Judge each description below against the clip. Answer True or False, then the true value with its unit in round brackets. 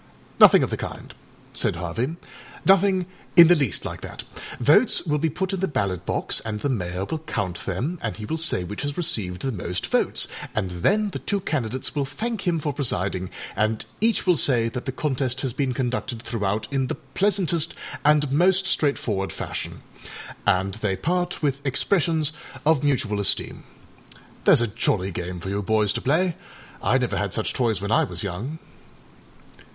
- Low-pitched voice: True (130 Hz)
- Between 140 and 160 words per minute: False (180 wpm)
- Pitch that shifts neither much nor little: False (7.8 semitones)